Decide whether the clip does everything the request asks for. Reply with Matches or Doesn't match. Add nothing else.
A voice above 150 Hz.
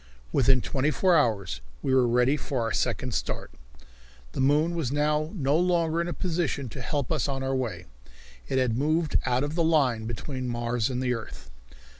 Doesn't match